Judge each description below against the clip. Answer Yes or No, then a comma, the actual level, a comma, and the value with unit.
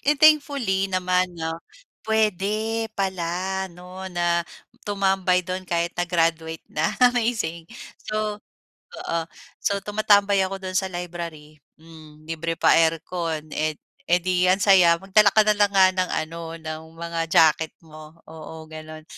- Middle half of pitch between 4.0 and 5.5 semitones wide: No, average, 3.1 semitones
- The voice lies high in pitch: No, medium, 180 Hz